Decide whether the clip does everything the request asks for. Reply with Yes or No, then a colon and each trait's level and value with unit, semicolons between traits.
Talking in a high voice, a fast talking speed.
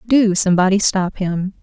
No: high, 195 Hz; average, 150 wpm